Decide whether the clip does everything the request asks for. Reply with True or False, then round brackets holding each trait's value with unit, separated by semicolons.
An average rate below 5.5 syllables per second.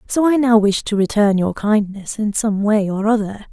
True (4.8 syllables/s)